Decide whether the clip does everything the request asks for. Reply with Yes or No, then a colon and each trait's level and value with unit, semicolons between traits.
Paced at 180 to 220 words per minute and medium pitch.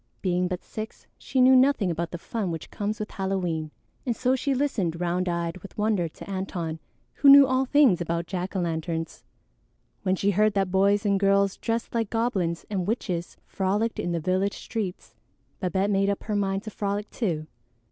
No: average, 190 wpm; high, 195 Hz